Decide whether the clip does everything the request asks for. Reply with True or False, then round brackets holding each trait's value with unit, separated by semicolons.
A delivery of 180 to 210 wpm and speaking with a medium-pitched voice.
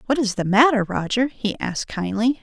False (200 wpm; 220 Hz)